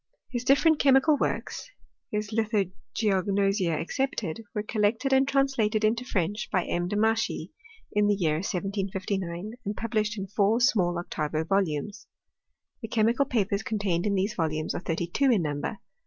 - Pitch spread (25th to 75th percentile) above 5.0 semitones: No, average, 3.6 semitones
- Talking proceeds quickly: No, average, 150 wpm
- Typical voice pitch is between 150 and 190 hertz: No, high, 205 Hz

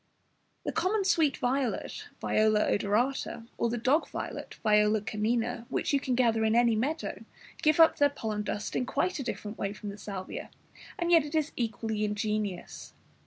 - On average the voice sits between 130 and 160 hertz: No, high, 230 Hz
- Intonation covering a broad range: No, average, 4.8 semitones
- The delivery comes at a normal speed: Yes, average, 170 wpm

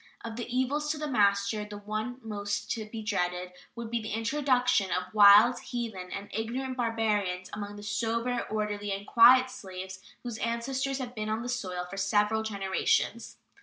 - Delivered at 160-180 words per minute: Yes, average, 170 wpm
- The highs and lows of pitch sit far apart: No, average, 3.0 semitones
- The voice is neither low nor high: No, high, 220 Hz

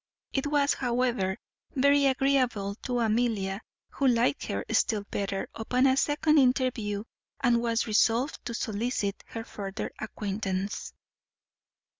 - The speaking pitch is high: Yes, high, 235 Hz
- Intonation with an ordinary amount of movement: Yes, average, 4.1 semitones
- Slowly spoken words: Yes, slow, 120 wpm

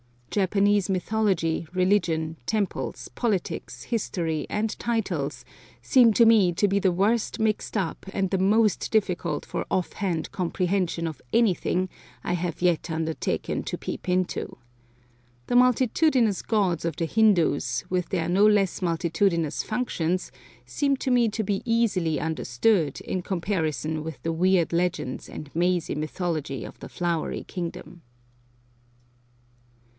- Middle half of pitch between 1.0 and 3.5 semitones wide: No, average, 4.1 semitones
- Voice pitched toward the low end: No, medium, 185 Hz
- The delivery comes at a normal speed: No, slow, 130 wpm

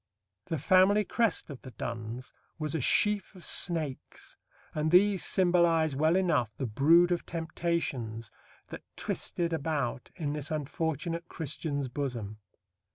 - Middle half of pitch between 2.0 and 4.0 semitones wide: No, average, 4.4 semitones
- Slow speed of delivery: Yes, slow, 130 wpm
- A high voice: No, medium, 160 Hz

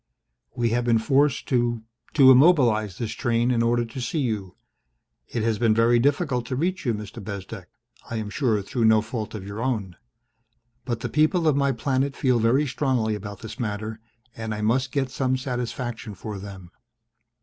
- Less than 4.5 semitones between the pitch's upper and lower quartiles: Yes, average, 3.2 semitones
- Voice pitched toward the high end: No, low, 115 Hz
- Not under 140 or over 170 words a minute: No, average, 185 wpm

